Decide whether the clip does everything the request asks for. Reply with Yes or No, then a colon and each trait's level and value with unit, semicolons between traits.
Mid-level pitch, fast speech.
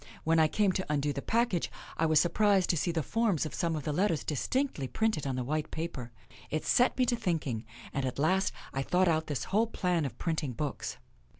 Yes: medium, 160 Hz; fast, 220 wpm